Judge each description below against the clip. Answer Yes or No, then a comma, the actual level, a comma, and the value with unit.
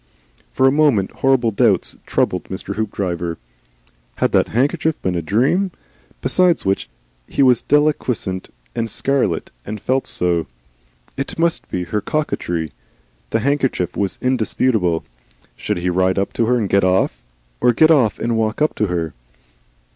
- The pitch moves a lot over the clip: Yes, wide, 6.5 semitones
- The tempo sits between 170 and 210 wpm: No, average, 150 wpm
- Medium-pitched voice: No, low, 110 Hz